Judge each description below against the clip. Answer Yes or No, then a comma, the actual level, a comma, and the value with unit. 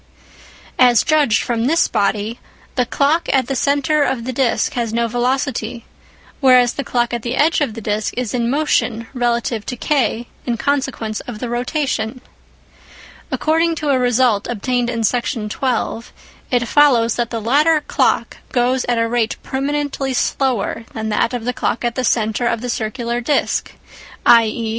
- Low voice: No, high, 245 Hz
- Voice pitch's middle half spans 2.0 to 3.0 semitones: Yes, average, 2.7 semitones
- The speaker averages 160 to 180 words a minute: Yes, average, 165 wpm